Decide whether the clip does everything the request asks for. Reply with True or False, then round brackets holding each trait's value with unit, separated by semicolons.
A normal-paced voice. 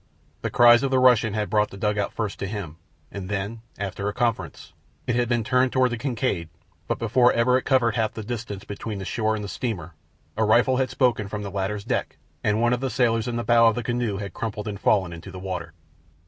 False (235 wpm)